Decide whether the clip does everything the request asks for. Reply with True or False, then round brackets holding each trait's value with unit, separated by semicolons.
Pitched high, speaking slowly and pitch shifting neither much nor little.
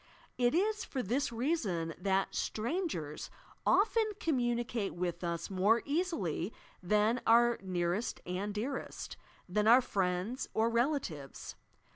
False (225 Hz; 120 wpm; 6.0 semitones)